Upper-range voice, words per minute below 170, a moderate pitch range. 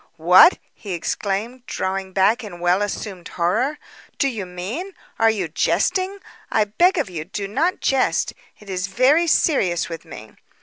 No: high, 200 Hz; average, 160 wpm; wide, 6.3 semitones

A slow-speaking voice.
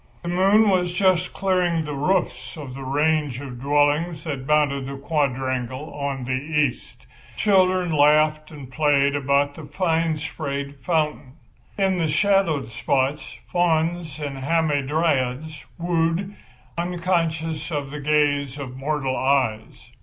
Yes: slow, 130 wpm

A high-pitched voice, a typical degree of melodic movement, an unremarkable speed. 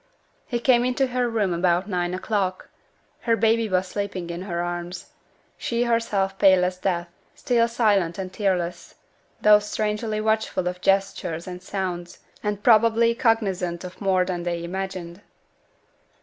Yes: high, 195 Hz; average, 3.6 semitones; average, 145 wpm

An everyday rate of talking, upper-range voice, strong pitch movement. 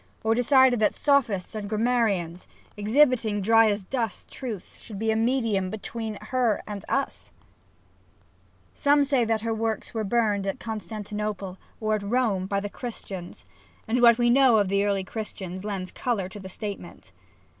No: average, 160 wpm; high, 215 Hz; average, 3.0 semitones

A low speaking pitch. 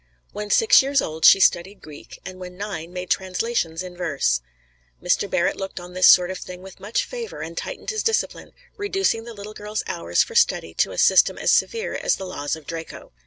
No: high, 190 Hz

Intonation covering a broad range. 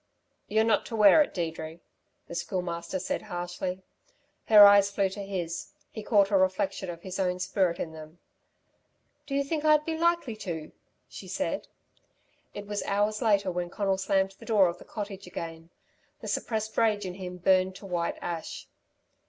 No: average, 2.9 semitones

